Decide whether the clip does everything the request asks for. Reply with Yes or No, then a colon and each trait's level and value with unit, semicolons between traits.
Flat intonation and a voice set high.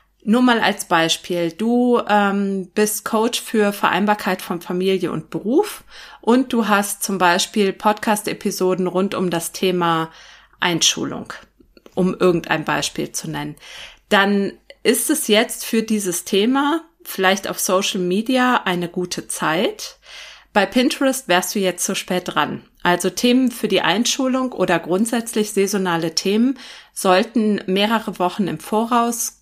No: average, 4.1 semitones; high, 200 Hz